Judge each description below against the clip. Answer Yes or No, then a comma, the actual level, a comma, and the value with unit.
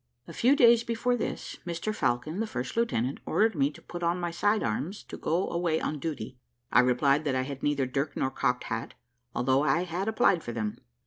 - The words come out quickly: Yes, fast, 210 wpm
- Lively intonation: Yes, wide, 6.8 semitones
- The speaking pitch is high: No, medium, 155 Hz